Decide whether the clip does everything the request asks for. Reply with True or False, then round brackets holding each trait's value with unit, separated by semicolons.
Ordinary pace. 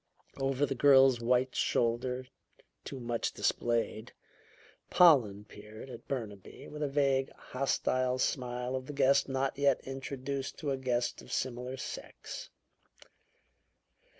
False (125 wpm)